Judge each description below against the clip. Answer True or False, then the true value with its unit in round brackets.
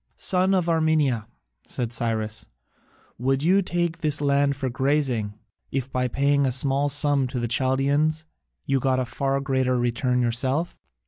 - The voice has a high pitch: False (135 Hz)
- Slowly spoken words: False (150 wpm)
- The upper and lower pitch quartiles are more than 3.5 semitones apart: False (2.6 semitones)